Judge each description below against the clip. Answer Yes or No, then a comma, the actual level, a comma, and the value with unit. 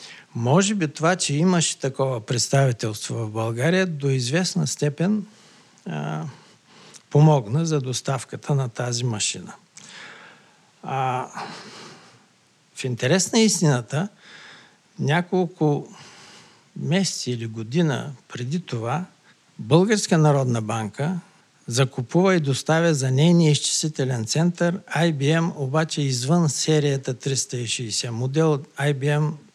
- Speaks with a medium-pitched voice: Yes, medium, 145 Hz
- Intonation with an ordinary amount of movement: Yes, average, 4.9 semitones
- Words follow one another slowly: Yes, slow, 95 wpm